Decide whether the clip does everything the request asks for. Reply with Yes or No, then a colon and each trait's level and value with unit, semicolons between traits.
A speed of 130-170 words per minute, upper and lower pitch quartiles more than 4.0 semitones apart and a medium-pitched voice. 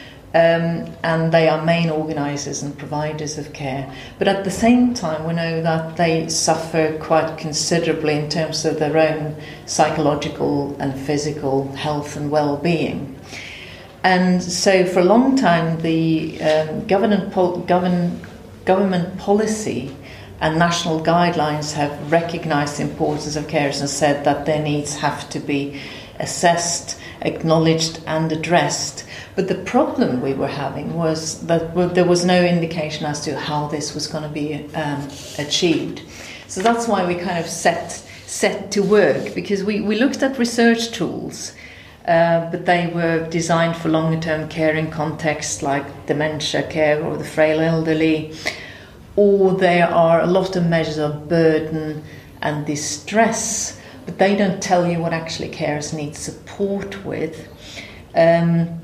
No: average, 150 wpm; average, 2.7 semitones; medium, 160 Hz